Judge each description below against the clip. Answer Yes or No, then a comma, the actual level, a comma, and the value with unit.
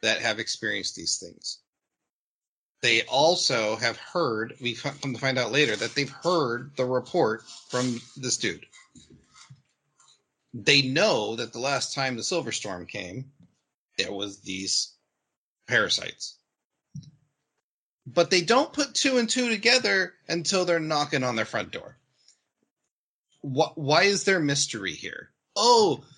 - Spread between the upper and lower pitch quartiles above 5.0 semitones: Yes, wide, 5.4 semitones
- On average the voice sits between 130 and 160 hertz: Yes, medium, 140 Hz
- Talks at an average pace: No, slow, 130 wpm